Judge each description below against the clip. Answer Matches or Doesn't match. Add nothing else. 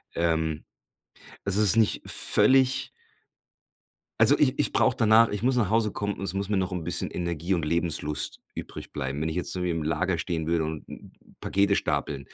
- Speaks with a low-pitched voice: Matches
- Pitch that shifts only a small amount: Doesn't match